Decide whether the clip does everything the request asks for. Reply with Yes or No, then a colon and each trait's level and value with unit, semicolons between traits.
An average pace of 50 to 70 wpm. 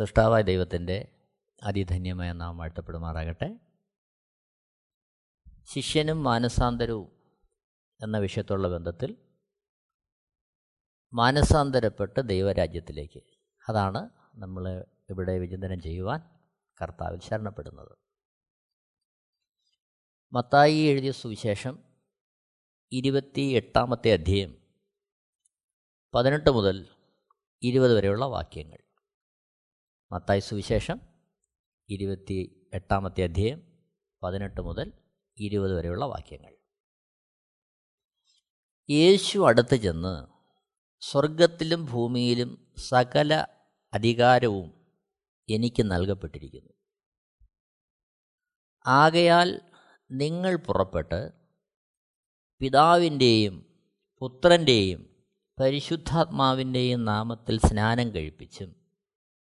Yes: slow, 60 wpm